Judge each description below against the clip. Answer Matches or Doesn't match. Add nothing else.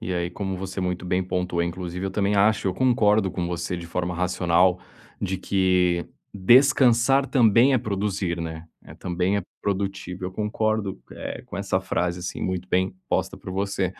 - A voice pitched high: Doesn't match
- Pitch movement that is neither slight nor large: Doesn't match